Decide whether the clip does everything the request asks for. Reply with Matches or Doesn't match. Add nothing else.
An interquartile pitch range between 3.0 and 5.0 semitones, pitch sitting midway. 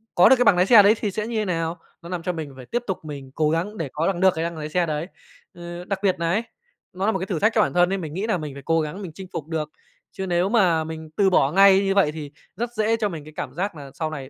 Matches